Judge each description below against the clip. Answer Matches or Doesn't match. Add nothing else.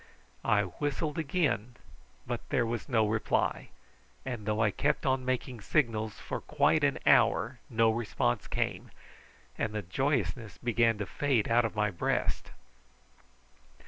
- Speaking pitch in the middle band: Doesn't match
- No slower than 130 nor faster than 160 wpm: Matches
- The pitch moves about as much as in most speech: Matches